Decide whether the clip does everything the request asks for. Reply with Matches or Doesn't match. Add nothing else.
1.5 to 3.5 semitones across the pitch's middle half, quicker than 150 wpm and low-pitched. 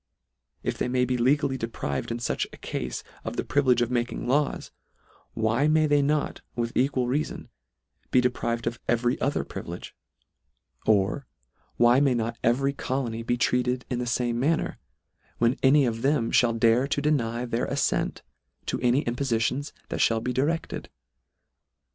Matches